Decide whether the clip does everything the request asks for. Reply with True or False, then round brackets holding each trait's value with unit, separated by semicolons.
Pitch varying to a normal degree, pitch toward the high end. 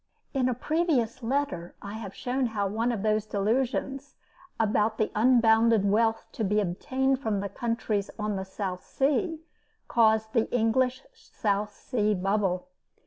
True (3.6 semitones; 220 Hz)